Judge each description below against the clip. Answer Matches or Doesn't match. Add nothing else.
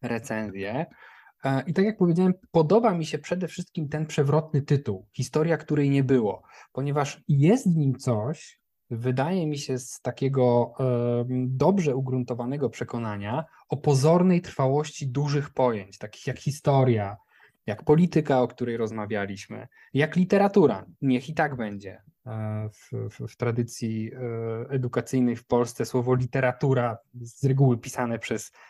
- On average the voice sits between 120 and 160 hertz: Matches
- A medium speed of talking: Matches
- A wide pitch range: Doesn't match